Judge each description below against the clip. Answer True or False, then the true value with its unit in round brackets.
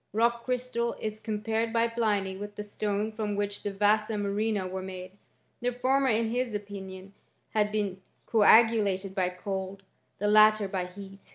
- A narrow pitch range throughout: True (2.3 semitones)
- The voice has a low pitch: False (210 Hz)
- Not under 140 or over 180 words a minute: True (160 wpm)